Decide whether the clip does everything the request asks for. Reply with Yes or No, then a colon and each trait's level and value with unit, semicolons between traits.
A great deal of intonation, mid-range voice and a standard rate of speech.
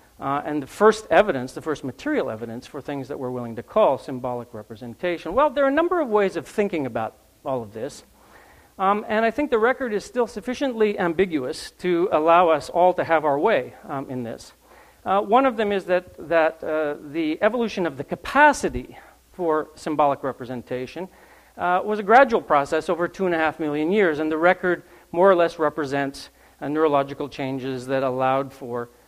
Yes: wide, 6.4 semitones; medium, 160 Hz; average, 190 wpm